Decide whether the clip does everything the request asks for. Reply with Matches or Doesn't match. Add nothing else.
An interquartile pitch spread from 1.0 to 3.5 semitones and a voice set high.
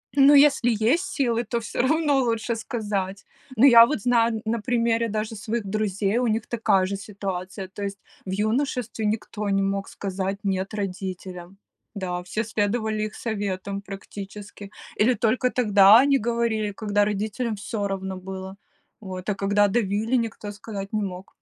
Matches